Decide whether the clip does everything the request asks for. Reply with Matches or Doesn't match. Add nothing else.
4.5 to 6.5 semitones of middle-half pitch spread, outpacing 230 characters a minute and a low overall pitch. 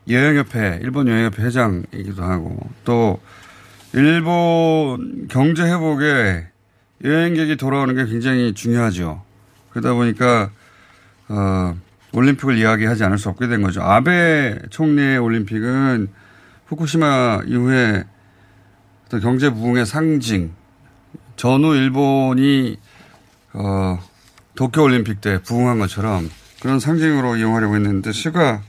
Matches